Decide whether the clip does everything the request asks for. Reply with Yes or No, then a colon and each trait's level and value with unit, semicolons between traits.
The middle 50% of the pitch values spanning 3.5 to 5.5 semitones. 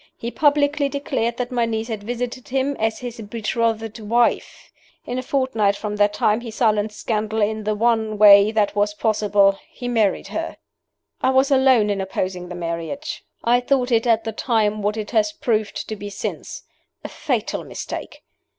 No: average, 2.8 semitones